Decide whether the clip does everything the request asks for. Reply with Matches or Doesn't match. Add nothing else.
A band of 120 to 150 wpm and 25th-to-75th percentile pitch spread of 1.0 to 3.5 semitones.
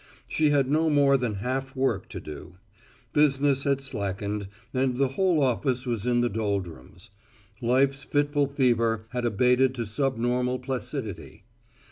Matches